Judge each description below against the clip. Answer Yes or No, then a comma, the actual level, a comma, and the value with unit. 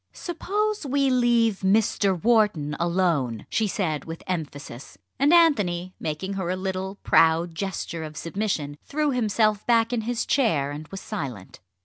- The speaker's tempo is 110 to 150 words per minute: Yes, average, 145 wpm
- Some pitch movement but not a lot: No, wide, 6.2 semitones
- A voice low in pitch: No, high, 190 Hz